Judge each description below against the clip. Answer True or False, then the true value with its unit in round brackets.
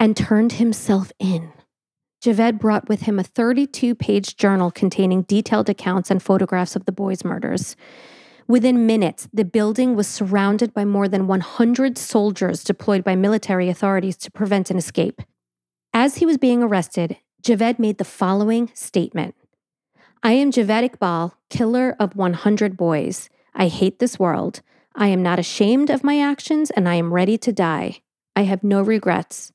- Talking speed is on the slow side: False (160 wpm)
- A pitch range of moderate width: True (3.7 semitones)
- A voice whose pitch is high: True (205 Hz)